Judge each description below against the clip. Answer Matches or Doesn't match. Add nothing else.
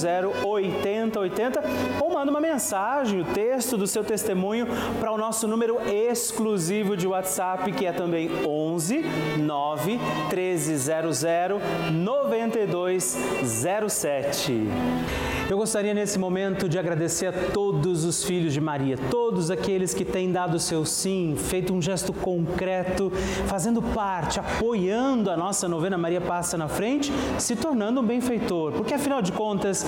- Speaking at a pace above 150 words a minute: Doesn't match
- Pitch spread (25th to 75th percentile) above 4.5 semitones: Doesn't match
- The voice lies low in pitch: Doesn't match